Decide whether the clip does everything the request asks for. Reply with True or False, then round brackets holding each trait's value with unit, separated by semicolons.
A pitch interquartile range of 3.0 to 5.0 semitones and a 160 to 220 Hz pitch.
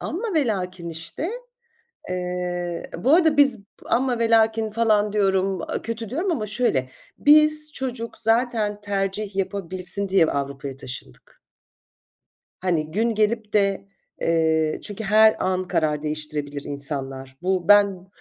False (5.4 semitones; 195 Hz)